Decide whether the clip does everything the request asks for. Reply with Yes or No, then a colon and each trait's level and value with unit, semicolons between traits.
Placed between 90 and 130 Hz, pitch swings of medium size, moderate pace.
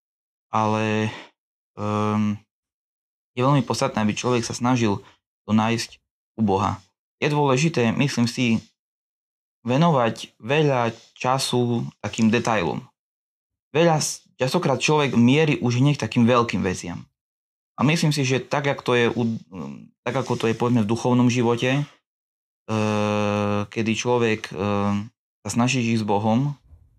Yes: low, 115 Hz; average, 3.2 semitones; average, 120 wpm